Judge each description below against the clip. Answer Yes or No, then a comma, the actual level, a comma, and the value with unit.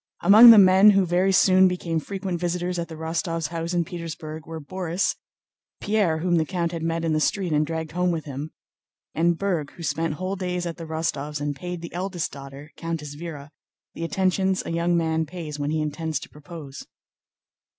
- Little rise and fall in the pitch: Yes, narrow, 2.3 semitones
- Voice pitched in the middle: Yes, medium, 165 Hz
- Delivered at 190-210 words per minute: Yes, average, 195 wpm